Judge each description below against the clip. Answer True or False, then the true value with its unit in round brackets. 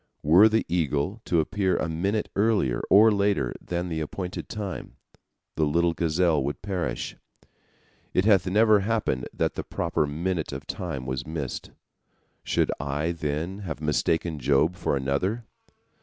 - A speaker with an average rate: True (145 wpm)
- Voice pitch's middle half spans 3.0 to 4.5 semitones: False (4.9 semitones)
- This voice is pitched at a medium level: False (85 Hz)